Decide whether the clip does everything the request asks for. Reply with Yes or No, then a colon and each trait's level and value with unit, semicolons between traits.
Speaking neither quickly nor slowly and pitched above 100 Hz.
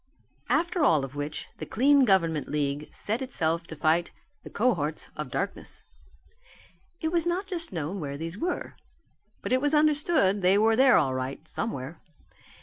Yes: average, 165 wpm; high, 190 Hz